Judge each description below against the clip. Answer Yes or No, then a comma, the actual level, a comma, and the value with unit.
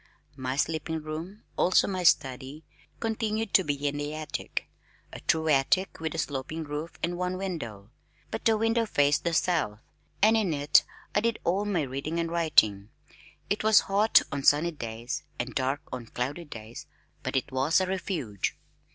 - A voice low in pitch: No, medium, 155 Hz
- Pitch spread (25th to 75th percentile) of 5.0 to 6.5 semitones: Yes, wide, 5.5 semitones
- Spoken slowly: No, average, 170 wpm